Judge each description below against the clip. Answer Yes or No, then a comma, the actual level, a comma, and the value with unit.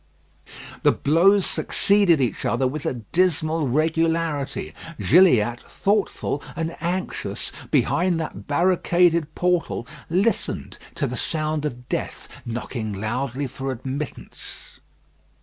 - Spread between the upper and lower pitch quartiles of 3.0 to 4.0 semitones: No, average, 4.9 semitones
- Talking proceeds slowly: Yes, slow, 105 wpm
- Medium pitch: Yes, medium, 155 Hz